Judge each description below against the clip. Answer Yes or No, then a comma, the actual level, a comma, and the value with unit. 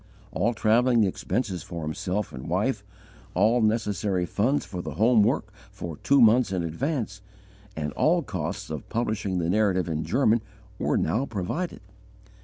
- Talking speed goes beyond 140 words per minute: Yes, average, 150 wpm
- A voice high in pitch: No, low, 105 Hz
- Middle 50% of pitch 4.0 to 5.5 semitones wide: Yes, average, 4.6 semitones